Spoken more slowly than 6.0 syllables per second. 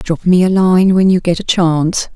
Yes: 4.8 syllables/s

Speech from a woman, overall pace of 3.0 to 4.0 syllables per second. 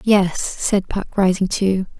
Yes: female; 3.5 syllables/s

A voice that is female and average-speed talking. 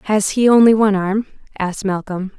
Yes: female; average, 175 wpm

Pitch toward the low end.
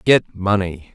Yes: low, 100 Hz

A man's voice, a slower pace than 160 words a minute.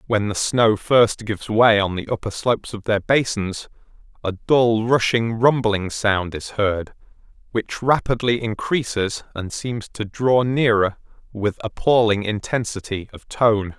Yes: male; average, 145 wpm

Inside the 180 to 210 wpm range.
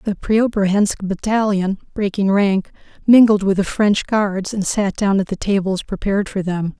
No: average, 170 wpm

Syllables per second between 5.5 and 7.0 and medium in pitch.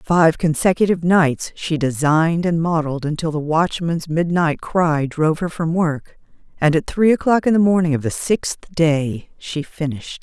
No: 4.6 syllables/s; medium, 165 Hz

